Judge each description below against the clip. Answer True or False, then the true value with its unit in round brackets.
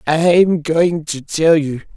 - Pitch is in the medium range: True (160 Hz)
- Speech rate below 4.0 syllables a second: True (3.5 syllables/s)